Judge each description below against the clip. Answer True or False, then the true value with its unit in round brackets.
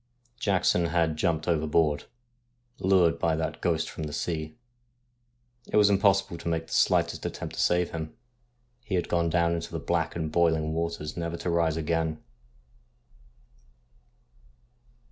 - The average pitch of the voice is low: True (85 Hz)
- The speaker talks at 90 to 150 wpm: True (145 wpm)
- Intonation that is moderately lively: False (1.6 semitones)